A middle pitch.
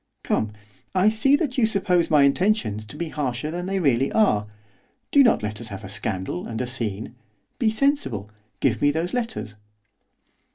Yes: medium, 150 Hz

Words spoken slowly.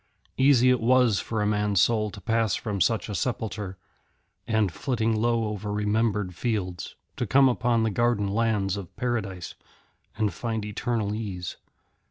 No: average, 155 wpm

